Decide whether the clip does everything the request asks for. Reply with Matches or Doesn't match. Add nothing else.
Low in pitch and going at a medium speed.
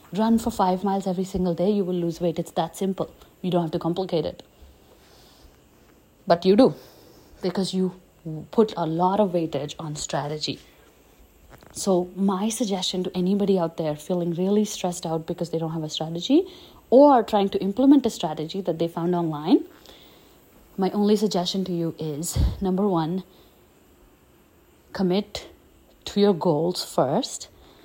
Doesn't match